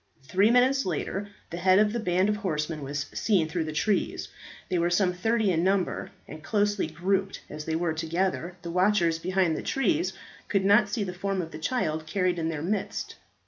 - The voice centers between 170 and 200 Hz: Yes, medium, 185 Hz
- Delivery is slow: No, average, 200 wpm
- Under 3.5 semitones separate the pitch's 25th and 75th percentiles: No, average, 3.8 semitones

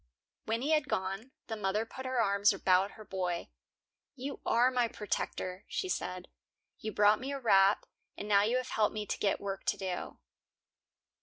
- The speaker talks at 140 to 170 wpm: No, average, 180 wpm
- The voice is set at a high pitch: Yes, high, 210 Hz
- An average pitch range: Yes, average, 4.1 semitones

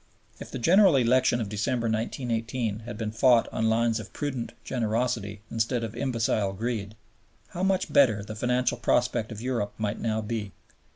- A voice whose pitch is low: Yes, low, 115 Hz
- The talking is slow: No, average, 165 wpm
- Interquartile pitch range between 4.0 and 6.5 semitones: No, narrow, 2.5 semitones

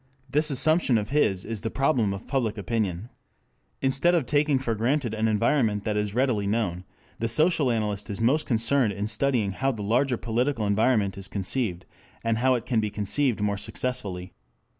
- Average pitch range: Yes, average, 4.4 semitones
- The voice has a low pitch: Yes, low, 115 Hz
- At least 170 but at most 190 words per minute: Yes, average, 180 wpm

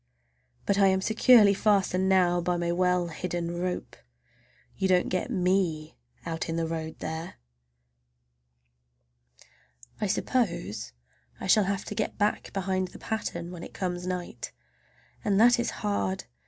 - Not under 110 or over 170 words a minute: Yes, average, 140 wpm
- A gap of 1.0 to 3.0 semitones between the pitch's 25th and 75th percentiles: Yes, narrow, 2.6 semitones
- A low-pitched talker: No, medium, 180 Hz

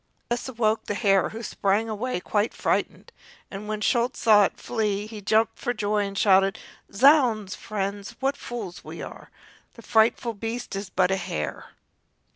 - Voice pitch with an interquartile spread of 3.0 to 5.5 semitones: No, narrow, 2.6 semitones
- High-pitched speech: Yes, high, 215 Hz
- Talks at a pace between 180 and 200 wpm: No, average, 165 wpm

